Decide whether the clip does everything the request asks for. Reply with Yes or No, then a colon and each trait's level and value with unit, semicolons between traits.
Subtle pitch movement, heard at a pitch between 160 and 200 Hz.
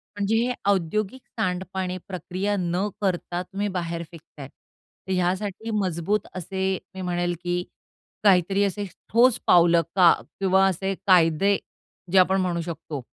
Yes: narrow, 2.2 semitones; medium, 185 Hz